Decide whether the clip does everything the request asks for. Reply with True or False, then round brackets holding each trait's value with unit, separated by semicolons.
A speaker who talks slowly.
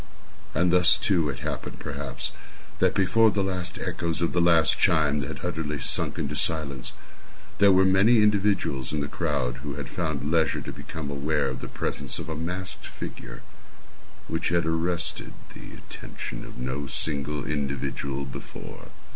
False (160 wpm)